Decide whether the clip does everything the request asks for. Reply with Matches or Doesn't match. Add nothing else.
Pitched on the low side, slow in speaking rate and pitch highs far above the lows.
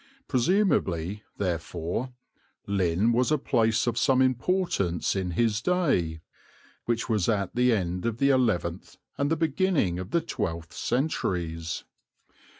Matches